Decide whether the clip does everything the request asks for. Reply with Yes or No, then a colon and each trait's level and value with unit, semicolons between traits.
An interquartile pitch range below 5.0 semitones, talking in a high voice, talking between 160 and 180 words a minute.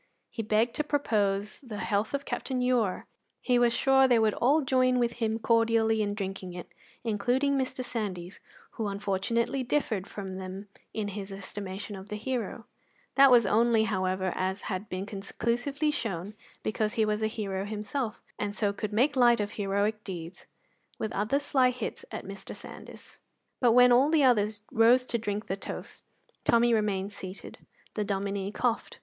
Yes: average, 3.5 semitones; high, 215 Hz; average, 170 wpm